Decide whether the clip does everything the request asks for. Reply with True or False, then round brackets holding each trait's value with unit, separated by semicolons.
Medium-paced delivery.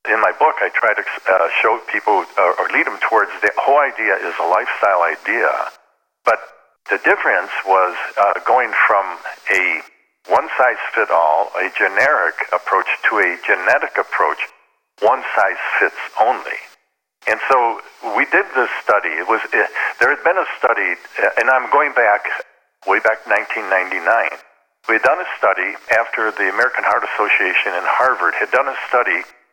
True (165 wpm)